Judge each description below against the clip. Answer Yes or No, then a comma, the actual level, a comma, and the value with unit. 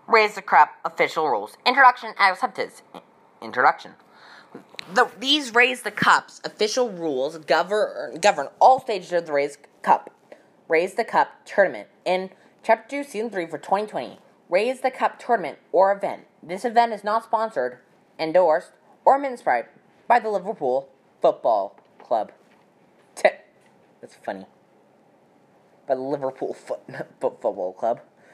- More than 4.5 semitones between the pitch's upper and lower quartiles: Yes, wide, 5.6 semitones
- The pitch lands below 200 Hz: No, high, 210 Hz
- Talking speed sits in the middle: No, slow, 125 wpm